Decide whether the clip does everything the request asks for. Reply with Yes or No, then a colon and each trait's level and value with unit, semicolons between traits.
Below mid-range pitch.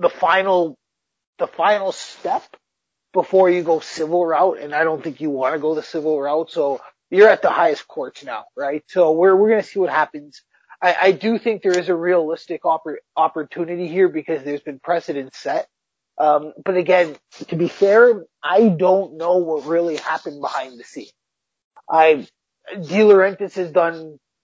No: medium, 170 Hz